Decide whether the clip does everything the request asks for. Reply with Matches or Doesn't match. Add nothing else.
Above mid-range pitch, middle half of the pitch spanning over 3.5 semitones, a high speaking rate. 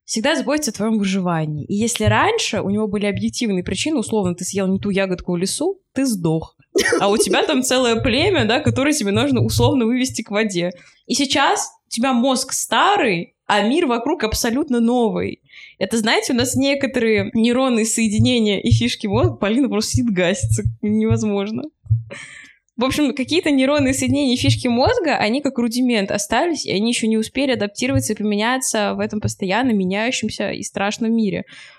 Matches